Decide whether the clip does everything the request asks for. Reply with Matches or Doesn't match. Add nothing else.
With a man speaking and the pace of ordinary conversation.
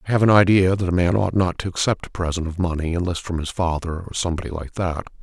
Doesn't match